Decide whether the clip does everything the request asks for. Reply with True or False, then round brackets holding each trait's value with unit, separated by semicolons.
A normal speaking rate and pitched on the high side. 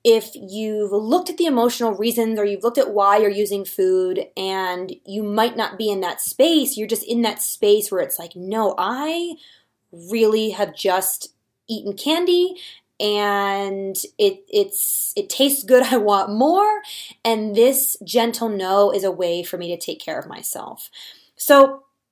True (170 wpm; 225 Hz)